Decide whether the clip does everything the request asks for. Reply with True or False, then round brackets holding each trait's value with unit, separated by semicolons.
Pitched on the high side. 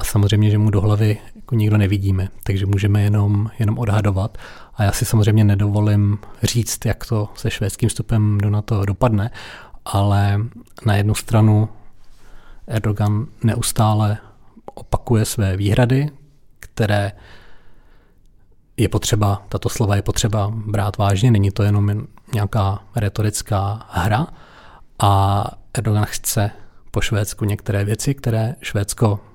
False (105 Hz)